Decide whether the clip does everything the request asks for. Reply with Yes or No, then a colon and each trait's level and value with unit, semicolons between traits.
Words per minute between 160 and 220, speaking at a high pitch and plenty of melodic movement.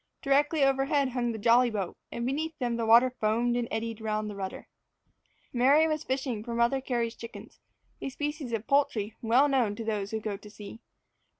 No: average, 195 wpm; high, 235 Hz; average, 3.6 semitones